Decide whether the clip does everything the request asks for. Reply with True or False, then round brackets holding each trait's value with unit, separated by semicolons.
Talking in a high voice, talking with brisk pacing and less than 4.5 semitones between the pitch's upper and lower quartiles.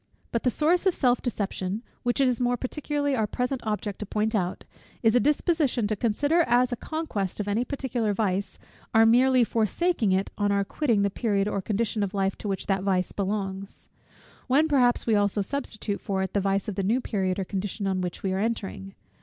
True (215 Hz; 210 wpm; 4.0 semitones)